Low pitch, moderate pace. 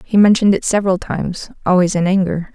No: high, 190 Hz; average, 190 wpm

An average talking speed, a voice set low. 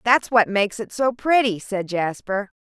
No: average, 180 wpm; high, 215 Hz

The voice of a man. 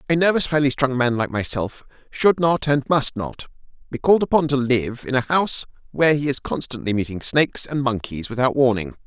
Yes: male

